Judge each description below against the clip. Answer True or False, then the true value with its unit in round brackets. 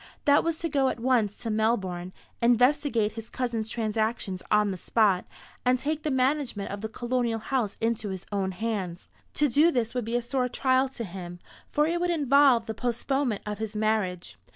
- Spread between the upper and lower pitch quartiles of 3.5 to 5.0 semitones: True (3.8 semitones)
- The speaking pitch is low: False (230 Hz)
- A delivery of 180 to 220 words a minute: True (190 wpm)